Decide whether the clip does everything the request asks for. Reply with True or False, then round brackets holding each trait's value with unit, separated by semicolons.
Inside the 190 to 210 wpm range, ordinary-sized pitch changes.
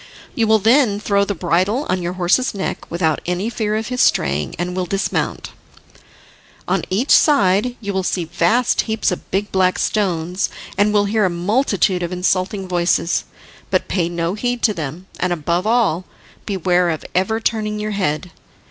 False (175 wpm; 3.4 semitones)